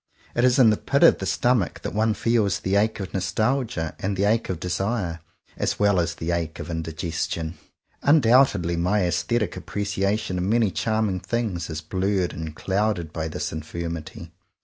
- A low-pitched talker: Yes, very low, 95 Hz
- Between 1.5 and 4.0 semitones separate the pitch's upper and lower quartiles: No, average, 4.5 semitones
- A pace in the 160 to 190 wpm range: Yes, average, 180 wpm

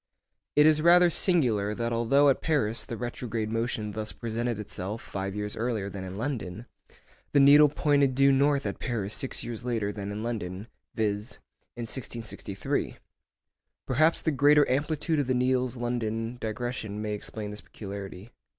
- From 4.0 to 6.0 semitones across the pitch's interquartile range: Yes, average, 4.5 semitones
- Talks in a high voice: No, low, 115 Hz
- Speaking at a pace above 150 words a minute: Yes, average, 160 wpm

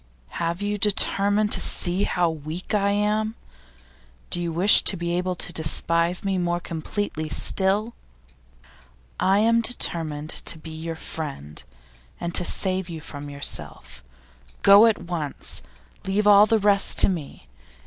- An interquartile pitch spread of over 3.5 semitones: Yes, average, 3.9 semitones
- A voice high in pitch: No, medium, 180 Hz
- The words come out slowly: No, average, 145 wpm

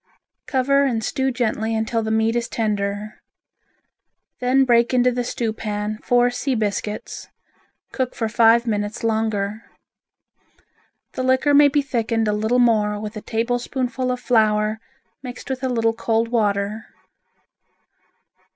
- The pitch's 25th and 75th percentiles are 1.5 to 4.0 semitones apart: Yes, narrow, 2.5 semitones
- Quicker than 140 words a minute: No, slow, 135 wpm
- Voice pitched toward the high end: Yes, high, 230 Hz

